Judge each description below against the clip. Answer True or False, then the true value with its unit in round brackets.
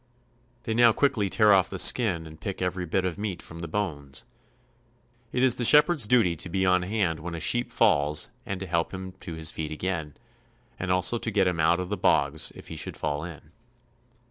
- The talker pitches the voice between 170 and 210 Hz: False (90 Hz)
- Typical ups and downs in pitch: True (4.3 semitones)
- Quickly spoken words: True (215 wpm)